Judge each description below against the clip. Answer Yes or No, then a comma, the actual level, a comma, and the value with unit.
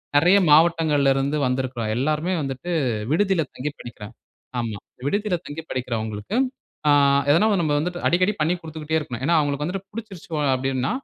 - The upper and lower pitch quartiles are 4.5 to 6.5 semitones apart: Yes, average, 4.9 semitones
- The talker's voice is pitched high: No, medium, 150 Hz